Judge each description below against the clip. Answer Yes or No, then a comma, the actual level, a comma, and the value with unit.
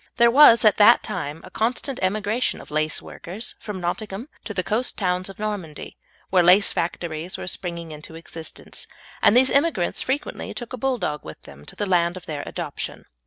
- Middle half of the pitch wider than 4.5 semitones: Yes, average, 5.1 semitones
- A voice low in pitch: No, high, 190 Hz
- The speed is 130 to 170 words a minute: No, average, 180 wpm